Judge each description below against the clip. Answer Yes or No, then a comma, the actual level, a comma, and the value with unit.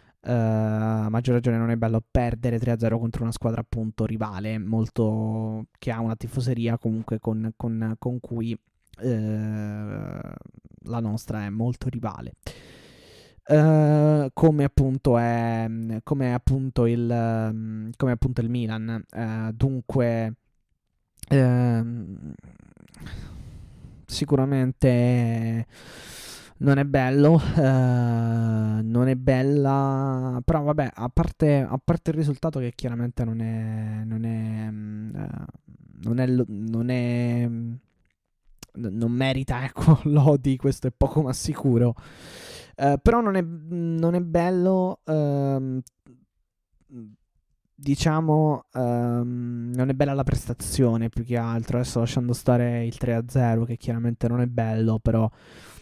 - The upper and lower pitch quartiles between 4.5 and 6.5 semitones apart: No, average, 3.1 semitones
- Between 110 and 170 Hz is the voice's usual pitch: Yes, low, 120 Hz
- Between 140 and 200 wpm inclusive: No, average, 125 wpm